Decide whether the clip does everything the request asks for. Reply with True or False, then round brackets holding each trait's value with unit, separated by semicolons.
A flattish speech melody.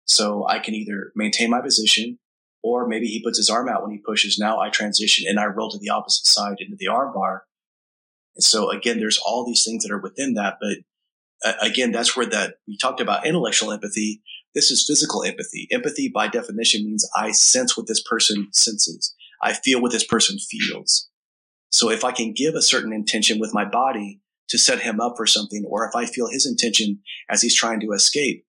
True (1.8 semitones)